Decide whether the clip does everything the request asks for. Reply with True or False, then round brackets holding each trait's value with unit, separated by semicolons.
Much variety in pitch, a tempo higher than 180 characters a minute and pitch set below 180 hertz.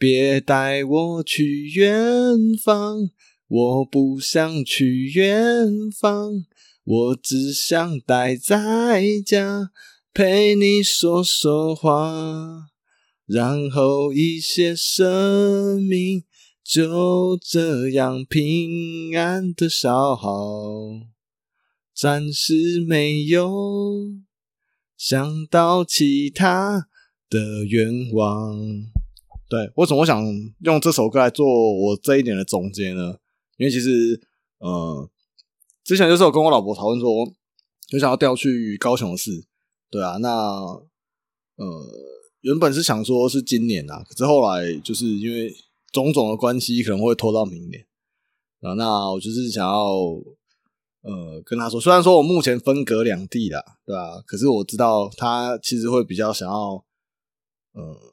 False (7.2 semitones; 170 characters per minute; 140 Hz)